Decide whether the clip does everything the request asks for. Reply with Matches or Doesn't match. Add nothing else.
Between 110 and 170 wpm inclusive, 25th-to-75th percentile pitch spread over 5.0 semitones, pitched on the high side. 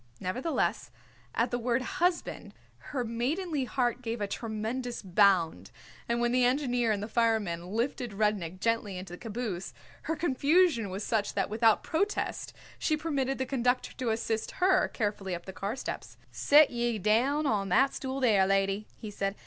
Doesn't match